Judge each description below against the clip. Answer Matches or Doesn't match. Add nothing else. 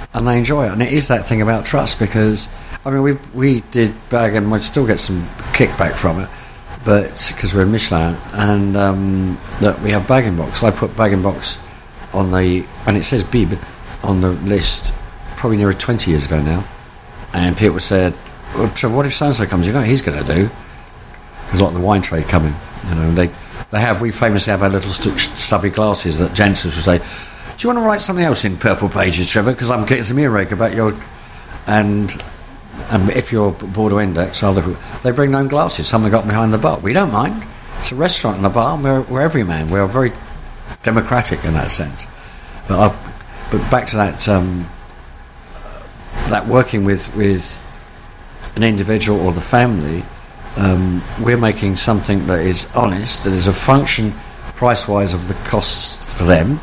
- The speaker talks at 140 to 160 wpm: Doesn't match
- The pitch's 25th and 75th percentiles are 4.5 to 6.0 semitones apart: Doesn't match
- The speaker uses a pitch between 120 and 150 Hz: Doesn't match